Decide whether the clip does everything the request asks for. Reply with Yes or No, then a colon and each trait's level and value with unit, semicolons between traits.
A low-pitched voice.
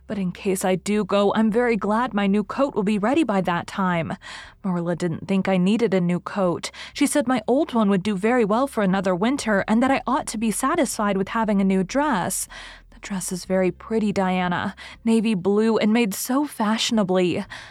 No: high, 210 Hz